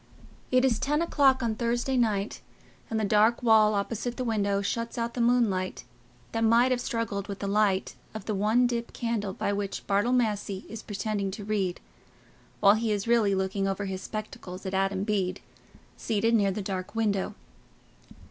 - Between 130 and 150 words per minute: No, average, 175 wpm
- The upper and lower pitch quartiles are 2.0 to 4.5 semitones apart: Yes, average, 2.8 semitones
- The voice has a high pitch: Yes, high, 215 Hz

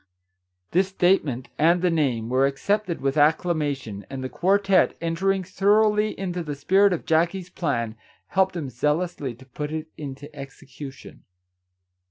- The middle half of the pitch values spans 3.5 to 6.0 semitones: Yes, wide, 5.4 semitones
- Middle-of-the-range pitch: Yes, medium, 155 Hz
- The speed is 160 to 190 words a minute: No, average, 145 wpm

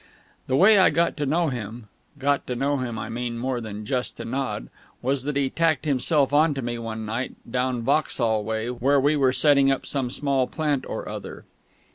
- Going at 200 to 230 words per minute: Yes, fast, 205 wpm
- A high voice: No, low, 130 Hz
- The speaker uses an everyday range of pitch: Yes, average, 3.3 semitones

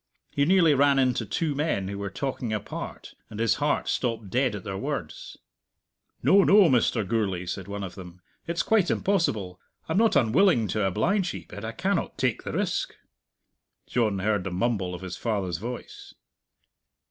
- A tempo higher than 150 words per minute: Yes, average, 170 wpm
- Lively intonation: Yes, wide, 6.8 semitones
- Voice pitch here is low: Yes, low, 115 Hz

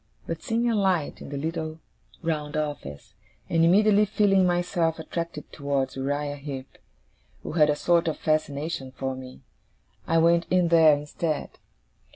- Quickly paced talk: No, average, 150 wpm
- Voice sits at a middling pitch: Yes, medium, 160 Hz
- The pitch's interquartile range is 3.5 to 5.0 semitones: No, average, 3.0 semitones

